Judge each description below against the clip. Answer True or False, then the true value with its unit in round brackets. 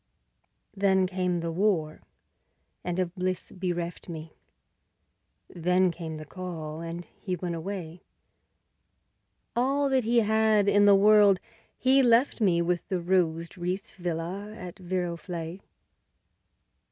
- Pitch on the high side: False (180 Hz)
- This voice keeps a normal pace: False (120 wpm)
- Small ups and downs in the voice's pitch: False (3.0 semitones)